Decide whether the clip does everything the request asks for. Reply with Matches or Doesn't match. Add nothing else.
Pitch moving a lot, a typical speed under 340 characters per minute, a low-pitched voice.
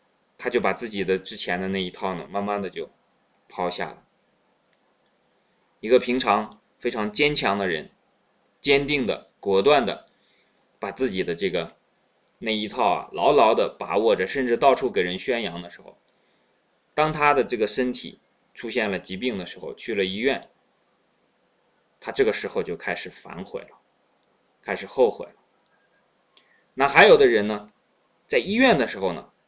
Matches